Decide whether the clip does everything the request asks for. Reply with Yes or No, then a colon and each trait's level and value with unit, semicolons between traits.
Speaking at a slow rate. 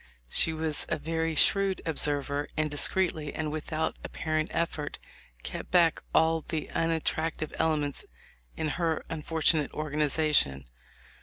Yes: slow, 125 wpm